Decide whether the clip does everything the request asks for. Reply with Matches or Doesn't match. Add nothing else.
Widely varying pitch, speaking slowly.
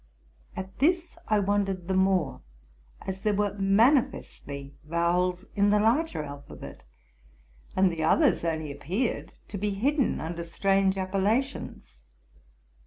Doesn't match